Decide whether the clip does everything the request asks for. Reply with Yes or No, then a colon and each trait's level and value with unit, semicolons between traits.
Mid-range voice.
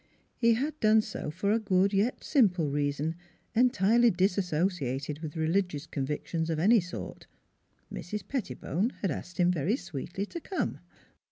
Yes: medium, 180 Hz